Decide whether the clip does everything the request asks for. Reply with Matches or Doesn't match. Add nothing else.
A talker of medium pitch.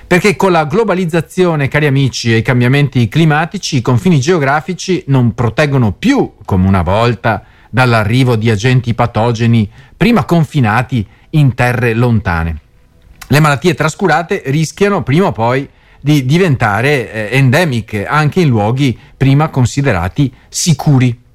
Doesn't match